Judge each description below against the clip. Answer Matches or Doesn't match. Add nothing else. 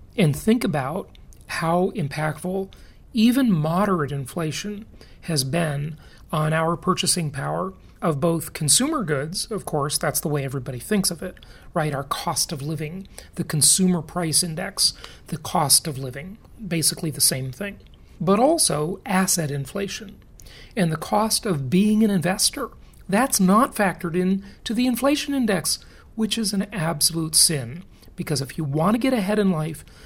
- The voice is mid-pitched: Matches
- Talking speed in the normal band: Matches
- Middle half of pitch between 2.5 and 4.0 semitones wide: Doesn't match